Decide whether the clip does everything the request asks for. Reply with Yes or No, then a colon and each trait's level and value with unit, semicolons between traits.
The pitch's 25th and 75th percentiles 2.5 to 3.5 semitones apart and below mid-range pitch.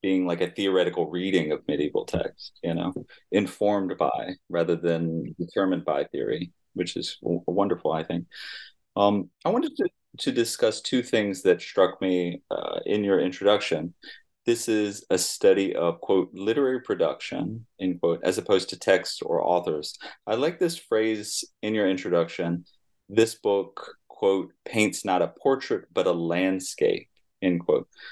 Yes: average, 3.0 semitones; low, 100 Hz